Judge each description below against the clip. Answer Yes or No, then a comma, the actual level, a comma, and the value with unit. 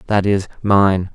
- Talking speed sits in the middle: Yes, average, 155 wpm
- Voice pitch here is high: No, low, 100 Hz